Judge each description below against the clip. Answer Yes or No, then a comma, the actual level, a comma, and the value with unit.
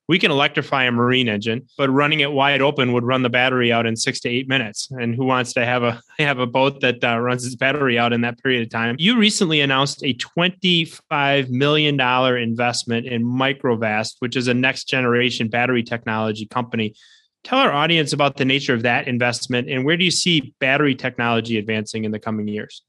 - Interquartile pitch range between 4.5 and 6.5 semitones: No, average, 2.9 semitones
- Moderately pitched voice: No, low, 125 Hz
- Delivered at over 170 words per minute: Yes, fast, 205 wpm